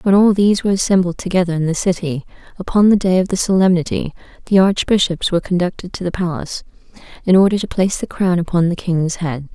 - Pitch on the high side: No, medium, 180 Hz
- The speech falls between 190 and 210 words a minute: Yes, average, 200 wpm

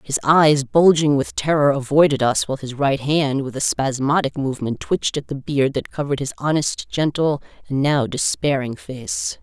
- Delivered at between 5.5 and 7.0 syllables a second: No, 4.9 syllables/s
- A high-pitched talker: No, medium, 140 Hz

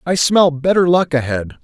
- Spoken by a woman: No, male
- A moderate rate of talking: Yes, average, 185 wpm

